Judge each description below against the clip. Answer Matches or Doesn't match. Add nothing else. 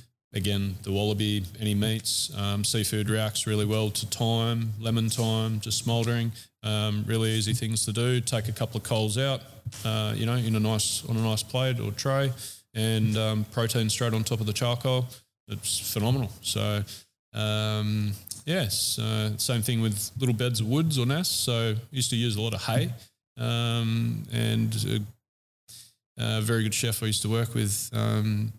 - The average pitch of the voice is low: Matches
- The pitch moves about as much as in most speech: Doesn't match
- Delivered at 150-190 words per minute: Matches